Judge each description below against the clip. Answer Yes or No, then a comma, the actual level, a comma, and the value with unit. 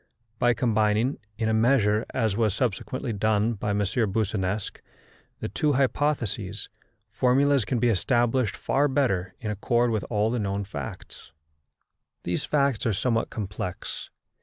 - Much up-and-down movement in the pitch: No, average, 3.4 semitones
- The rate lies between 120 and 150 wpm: Yes, slow, 135 wpm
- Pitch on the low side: Yes, low, 110 Hz